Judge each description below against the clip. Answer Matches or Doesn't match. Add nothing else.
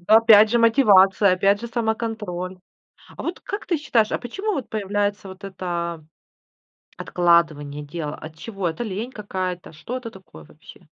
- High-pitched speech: Matches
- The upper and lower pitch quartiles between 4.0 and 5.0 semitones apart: Matches